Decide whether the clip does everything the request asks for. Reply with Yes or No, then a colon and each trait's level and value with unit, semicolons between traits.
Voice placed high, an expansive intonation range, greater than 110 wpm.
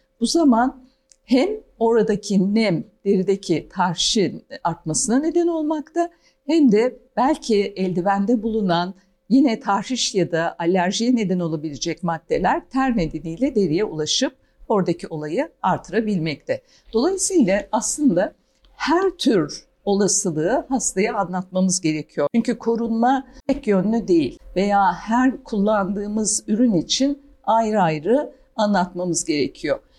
No: high, 215 Hz; wide, 6.1 semitones; average, 105 wpm